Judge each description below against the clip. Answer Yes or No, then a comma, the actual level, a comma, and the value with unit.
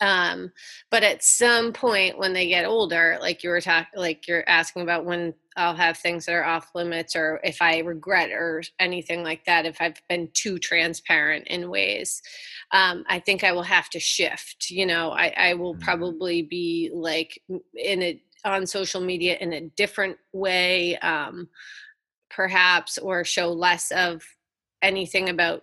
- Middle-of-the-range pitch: Yes, medium, 175 Hz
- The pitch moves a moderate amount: No, narrow, 2.1 semitones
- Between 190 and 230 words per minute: No, average, 170 wpm